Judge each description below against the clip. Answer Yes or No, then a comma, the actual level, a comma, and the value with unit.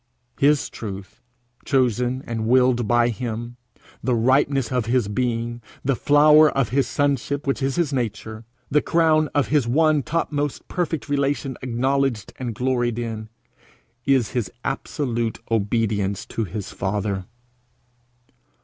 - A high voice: No, low, 125 Hz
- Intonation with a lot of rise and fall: No, average, 3.6 semitones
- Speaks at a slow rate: Yes, slow, 130 wpm